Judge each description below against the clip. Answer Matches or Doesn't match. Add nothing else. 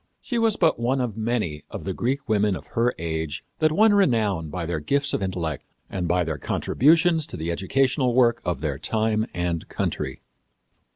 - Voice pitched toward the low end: Matches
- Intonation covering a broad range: Matches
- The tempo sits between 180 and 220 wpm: Matches